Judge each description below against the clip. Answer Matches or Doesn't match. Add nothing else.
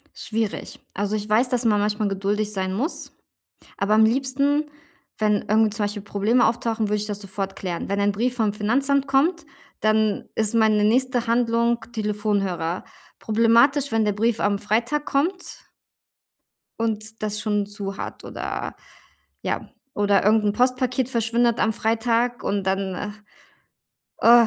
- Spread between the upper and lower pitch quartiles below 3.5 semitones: Matches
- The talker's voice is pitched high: Matches